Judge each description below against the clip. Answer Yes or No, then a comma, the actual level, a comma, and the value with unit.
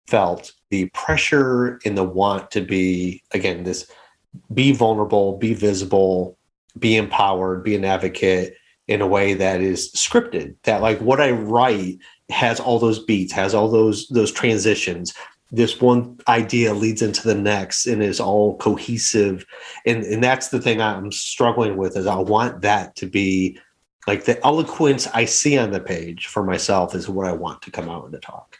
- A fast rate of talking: No, average, 175 wpm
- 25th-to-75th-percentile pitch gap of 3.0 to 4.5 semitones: Yes, average, 3.3 semitones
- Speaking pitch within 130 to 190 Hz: No, low, 105 Hz